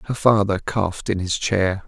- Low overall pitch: Yes, low, 100 Hz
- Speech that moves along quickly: No, average, 190 wpm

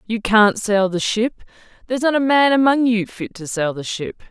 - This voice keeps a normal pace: No, fast, 210 wpm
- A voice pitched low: No, high, 220 Hz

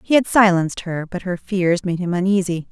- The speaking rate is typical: No, fast, 220 wpm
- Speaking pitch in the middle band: Yes, medium, 180 Hz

